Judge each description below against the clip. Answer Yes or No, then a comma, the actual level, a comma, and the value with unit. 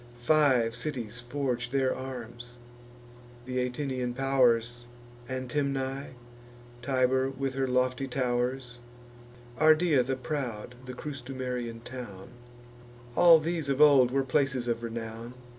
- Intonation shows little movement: Yes, narrow, 2.0 semitones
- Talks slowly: Yes, slow, 110 wpm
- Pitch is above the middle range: No, low, 130 Hz